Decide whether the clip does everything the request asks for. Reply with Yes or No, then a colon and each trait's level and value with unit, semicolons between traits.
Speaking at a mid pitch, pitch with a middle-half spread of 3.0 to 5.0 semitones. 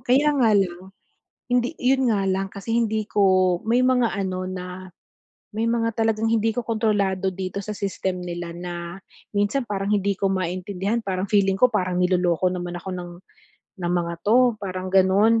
No: high, 195 Hz; average, 3.4 semitones